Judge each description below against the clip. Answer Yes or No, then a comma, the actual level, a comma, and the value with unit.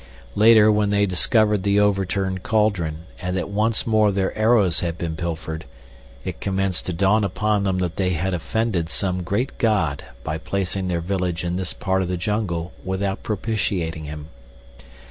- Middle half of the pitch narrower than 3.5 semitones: Yes, average, 3.1 semitones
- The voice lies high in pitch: No, very low, 95 Hz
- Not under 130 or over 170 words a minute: Yes, average, 165 wpm